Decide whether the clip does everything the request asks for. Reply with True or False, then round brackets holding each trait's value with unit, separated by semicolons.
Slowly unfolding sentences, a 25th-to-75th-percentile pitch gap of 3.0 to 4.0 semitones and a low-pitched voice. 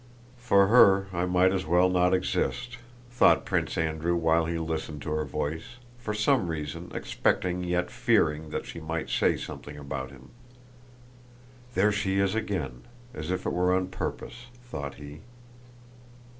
False (155 wpm; 3.7 semitones; 90 Hz)